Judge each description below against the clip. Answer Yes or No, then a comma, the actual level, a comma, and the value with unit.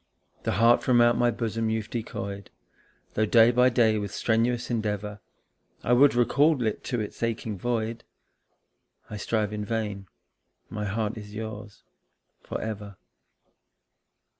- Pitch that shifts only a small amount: Yes, narrow, 2.2 semitones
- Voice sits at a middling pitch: No, low, 110 Hz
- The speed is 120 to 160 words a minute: Yes, average, 140 wpm